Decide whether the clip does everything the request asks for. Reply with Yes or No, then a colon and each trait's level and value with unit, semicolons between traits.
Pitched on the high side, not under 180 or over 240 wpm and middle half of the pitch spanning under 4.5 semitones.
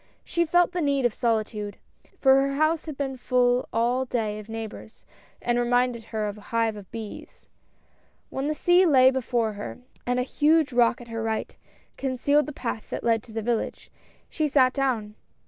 Yes: high, 245 Hz; average, 190 wpm; average, 3.6 semitones